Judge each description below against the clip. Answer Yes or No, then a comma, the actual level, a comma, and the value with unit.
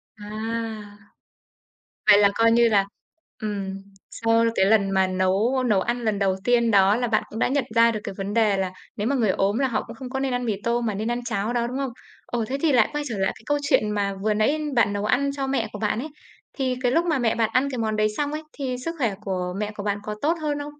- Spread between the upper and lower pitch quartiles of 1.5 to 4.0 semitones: Yes, average, 3.5 semitones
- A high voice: Yes, high, 225 Hz